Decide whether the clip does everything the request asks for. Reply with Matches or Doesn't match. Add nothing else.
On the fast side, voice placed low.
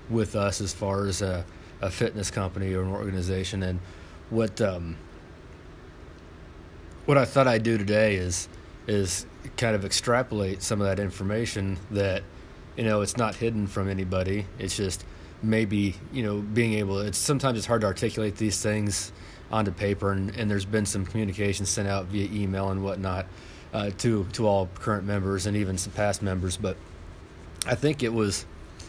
Doesn't match